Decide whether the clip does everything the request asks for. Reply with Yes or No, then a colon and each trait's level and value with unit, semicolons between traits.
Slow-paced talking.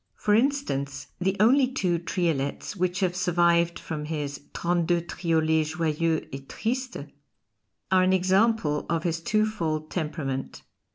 Yes: slow, 130 wpm